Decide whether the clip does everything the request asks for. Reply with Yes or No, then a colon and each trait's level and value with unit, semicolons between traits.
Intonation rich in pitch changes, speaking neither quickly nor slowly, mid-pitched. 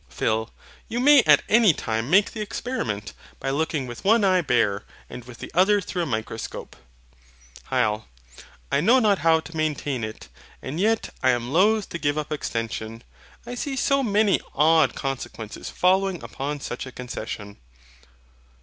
Yes: wide, 9.0 semitones; average, 160 wpm; medium, 150 Hz